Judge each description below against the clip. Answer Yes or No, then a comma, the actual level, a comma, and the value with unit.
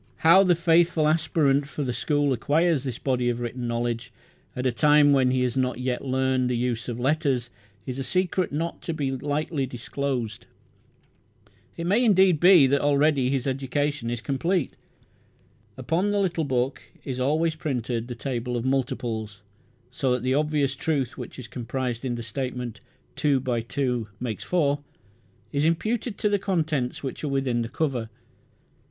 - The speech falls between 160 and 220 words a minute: Yes, average, 170 wpm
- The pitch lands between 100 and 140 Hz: Yes, low, 135 Hz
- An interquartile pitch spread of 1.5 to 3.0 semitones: No, average, 3.9 semitones